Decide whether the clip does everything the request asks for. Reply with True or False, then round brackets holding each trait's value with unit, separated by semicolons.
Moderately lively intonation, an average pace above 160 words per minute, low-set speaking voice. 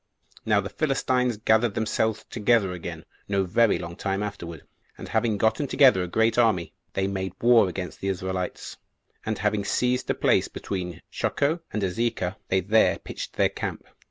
True (3.7 semitones; 170 wpm; 105 Hz)